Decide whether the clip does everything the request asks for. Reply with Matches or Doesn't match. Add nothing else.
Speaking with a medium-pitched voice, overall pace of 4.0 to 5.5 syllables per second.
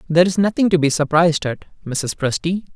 Matches